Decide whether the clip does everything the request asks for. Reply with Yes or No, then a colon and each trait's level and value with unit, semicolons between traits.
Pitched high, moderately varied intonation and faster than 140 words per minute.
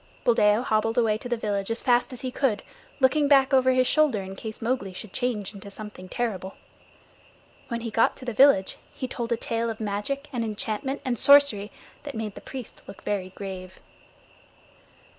Yes: high, 230 Hz; average, 3.8 semitones; average, 185 wpm